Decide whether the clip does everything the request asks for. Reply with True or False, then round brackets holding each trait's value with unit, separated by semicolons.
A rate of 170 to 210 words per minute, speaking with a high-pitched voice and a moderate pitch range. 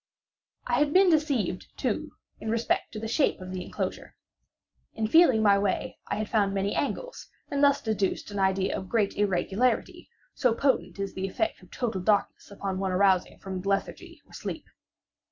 True (175 wpm; 205 Hz; 4.4 semitones)